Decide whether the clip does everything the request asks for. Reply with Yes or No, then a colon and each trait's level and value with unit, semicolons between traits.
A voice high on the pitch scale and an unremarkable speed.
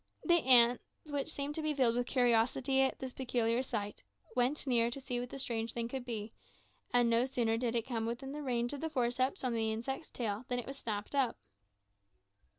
No: high, 245 Hz; fast, 210 wpm